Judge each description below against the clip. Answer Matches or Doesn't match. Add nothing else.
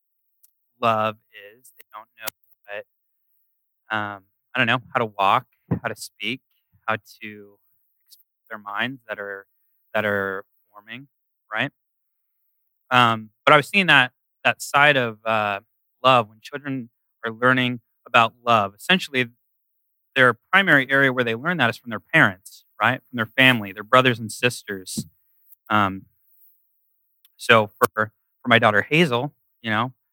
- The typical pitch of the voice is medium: Doesn't match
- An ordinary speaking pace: Matches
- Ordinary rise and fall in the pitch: Matches